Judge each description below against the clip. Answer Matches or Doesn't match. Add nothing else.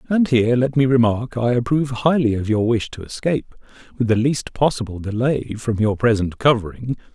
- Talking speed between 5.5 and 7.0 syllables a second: Matches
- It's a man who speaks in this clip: Matches